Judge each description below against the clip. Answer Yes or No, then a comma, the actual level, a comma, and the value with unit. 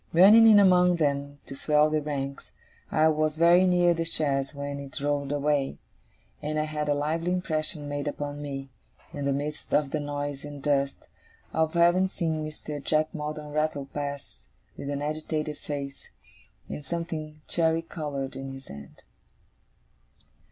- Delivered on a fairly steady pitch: Yes, narrow, 2.0 semitones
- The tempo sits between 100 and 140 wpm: No, average, 160 wpm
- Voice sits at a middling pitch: Yes, medium, 150 Hz